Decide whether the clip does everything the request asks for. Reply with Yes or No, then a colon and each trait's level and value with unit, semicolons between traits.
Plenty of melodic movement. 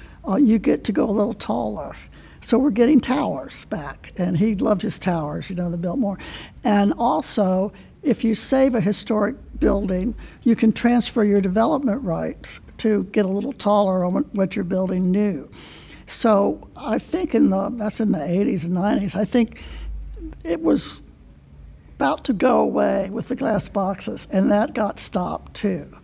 No: average, 3.6 semitones